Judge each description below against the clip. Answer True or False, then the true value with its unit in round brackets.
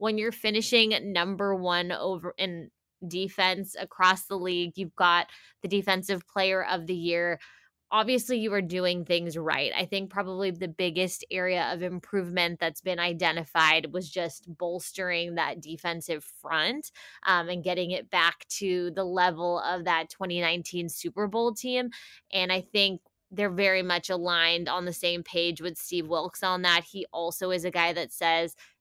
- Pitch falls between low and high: True (180 Hz)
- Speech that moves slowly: False (165 wpm)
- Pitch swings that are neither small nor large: False (1.9 semitones)